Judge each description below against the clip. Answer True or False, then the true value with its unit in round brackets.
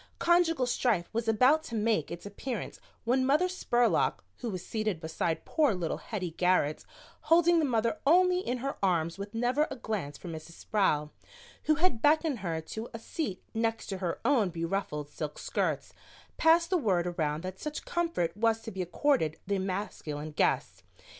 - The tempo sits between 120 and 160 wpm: False (175 wpm)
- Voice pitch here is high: True (220 Hz)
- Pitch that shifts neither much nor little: False (8.1 semitones)